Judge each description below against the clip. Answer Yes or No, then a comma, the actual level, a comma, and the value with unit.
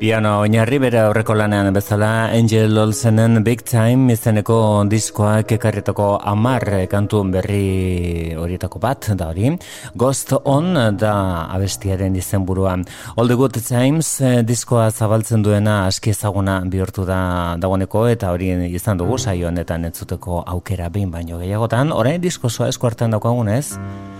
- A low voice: Yes, low, 105 Hz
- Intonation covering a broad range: No, average, 3.3 semitones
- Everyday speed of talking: Yes, average, 135 wpm